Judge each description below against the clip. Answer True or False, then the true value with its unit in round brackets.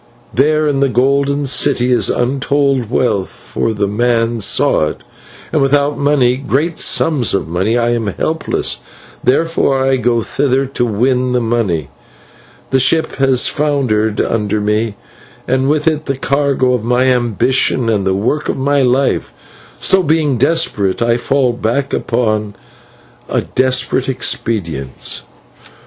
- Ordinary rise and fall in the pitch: True (3.4 semitones)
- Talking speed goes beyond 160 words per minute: False (140 wpm)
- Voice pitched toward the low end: True (125 Hz)